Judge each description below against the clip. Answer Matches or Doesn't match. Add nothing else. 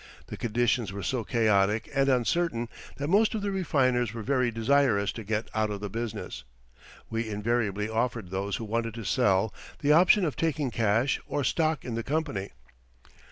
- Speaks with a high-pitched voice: Doesn't match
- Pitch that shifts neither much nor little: Matches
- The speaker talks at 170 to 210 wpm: Matches